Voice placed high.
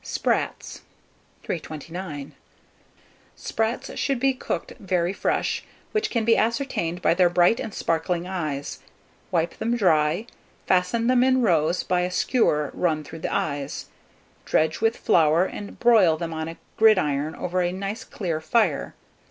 No: medium, 180 Hz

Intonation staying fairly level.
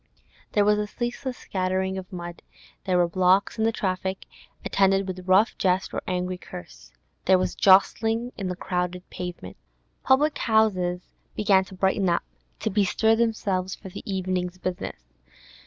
Yes: narrow, 2.3 semitones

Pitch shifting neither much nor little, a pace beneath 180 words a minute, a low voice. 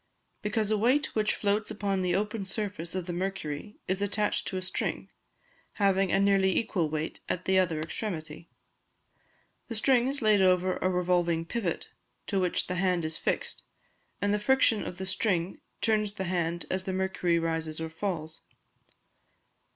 No: average, 3.2 semitones; average, 170 wpm; high, 190 Hz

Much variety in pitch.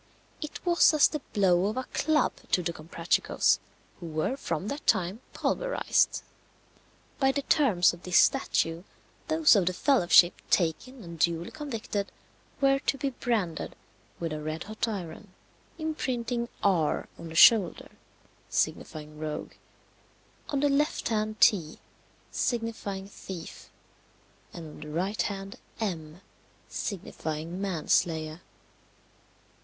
Yes: wide, 6.7 semitones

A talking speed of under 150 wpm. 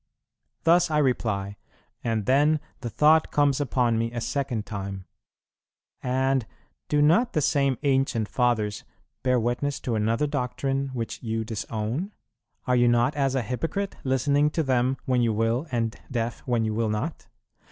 No: average, 155 wpm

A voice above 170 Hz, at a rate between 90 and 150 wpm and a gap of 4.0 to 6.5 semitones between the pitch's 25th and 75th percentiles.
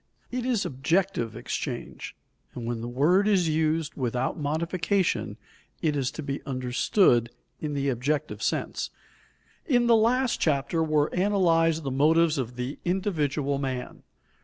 No: medium, 155 Hz; slow, 135 wpm; average, 5.1 semitones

